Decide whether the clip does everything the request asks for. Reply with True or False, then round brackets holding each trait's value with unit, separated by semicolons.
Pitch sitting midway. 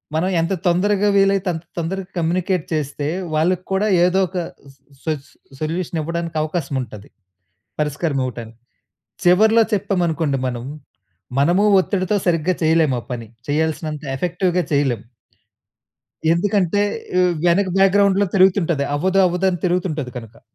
True (170 Hz)